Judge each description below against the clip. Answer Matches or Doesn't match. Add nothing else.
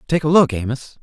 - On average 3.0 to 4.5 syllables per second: Doesn't match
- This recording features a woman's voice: Doesn't match